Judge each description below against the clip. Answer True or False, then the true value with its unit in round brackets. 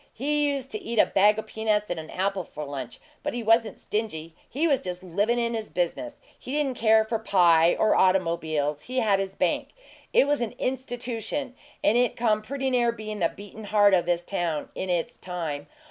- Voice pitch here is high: True (215 Hz)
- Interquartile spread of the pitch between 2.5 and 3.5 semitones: False (5.3 semitones)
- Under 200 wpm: False (205 wpm)